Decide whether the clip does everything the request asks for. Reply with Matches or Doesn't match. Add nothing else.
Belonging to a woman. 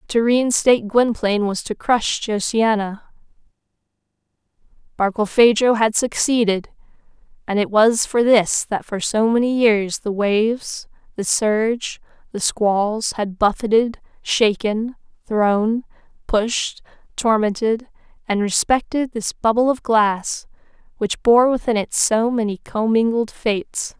Matches